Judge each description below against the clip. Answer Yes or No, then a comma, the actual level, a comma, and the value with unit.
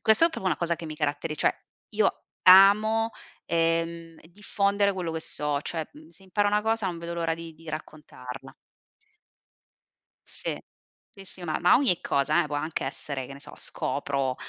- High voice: No, medium, 165 Hz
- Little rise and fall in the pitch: No, average, 4.1 semitones